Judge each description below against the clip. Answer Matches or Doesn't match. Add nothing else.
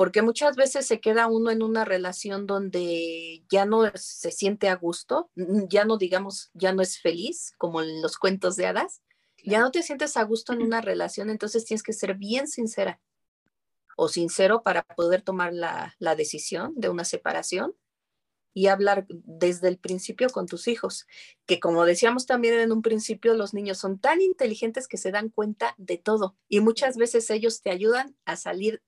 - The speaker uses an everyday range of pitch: Matches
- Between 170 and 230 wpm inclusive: Matches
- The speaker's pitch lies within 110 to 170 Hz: Doesn't match